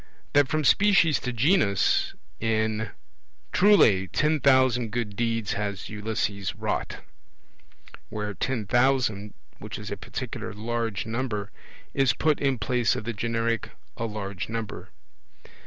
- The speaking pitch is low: Yes, low, 115 Hz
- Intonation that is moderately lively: Yes, average, 3.7 semitones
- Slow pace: Yes, slow, 125 wpm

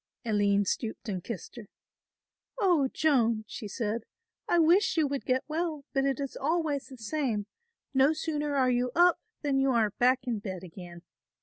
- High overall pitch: Yes, very high, 260 Hz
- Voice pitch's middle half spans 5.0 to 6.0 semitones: Yes, wide, 5.4 semitones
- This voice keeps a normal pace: Yes, average, 175 wpm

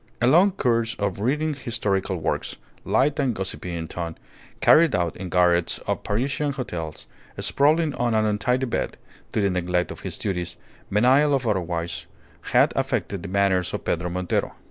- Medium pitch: No, low, 105 Hz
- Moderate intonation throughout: No, wide, 6.6 semitones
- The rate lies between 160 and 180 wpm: Yes, average, 165 wpm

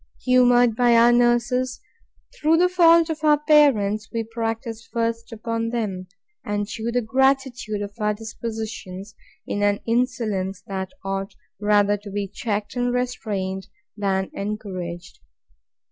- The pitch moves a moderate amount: Yes, average, 3.3 semitones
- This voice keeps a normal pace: No, slow, 130 wpm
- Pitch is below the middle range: No, high, 225 Hz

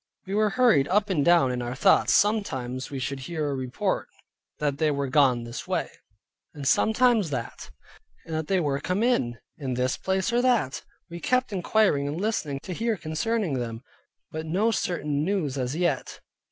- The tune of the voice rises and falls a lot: Yes, wide, 7.0 semitones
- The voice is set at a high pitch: No, medium, 155 Hz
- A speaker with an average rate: Yes, average, 180 wpm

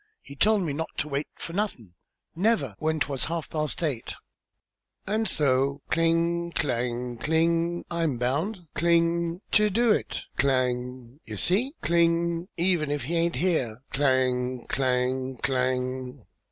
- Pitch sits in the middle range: Yes, medium, 150 Hz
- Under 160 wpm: Yes, average, 140 wpm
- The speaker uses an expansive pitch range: No, average, 4.9 semitones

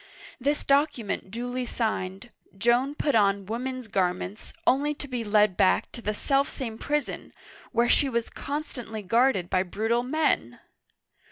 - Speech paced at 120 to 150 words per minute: Yes, average, 145 wpm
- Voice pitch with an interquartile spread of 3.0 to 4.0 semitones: No, average, 4.4 semitones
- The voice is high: Yes, high, 235 Hz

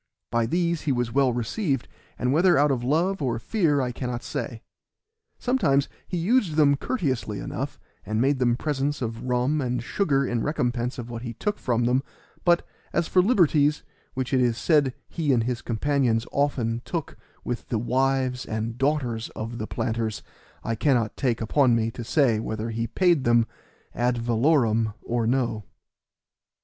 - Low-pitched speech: Yes, low, 125 Hz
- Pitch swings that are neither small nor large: Yes, average, 4.0 semitones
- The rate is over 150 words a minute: Yes, average, 170 wpm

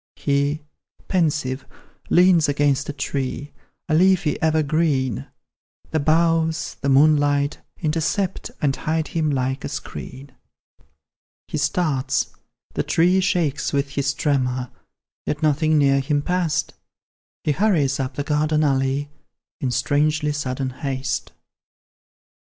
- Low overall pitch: No, medium, 145 Hz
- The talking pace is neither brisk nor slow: No, slow, 115 wpm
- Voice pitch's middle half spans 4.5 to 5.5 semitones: No, narrow, 2.5 semitones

